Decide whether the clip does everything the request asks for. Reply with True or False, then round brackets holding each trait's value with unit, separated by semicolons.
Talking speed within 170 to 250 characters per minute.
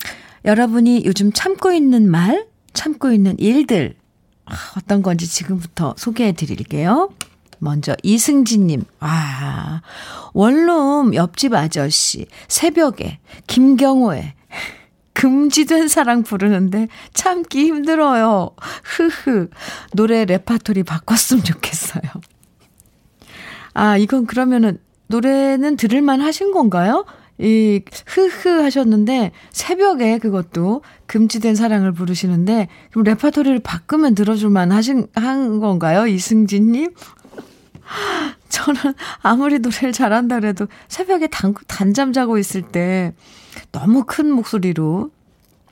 True (240 characters per minute)